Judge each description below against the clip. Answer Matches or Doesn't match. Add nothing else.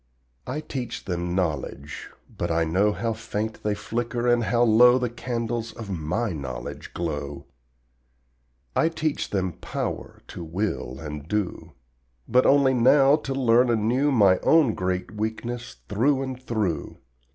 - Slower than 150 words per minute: Matches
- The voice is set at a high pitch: Doesn't match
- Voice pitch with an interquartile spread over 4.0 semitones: Matches